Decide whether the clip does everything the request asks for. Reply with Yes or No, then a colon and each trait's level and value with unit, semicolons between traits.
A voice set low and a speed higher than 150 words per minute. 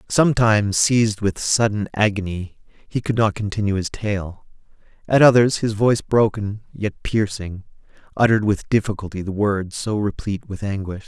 No: low, 105 Hz; average, 145 wpm